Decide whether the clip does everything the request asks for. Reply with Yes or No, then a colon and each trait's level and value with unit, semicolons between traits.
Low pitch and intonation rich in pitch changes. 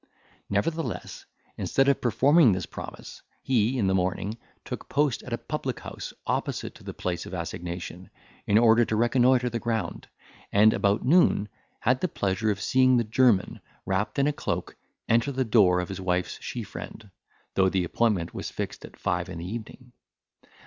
No: low, 110 Hz; average, 4.9 semitones